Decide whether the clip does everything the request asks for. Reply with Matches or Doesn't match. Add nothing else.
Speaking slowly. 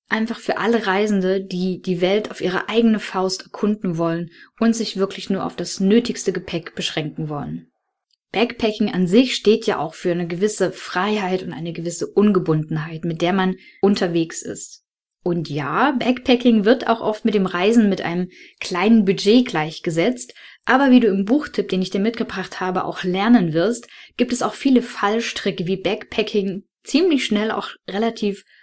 Doesn't match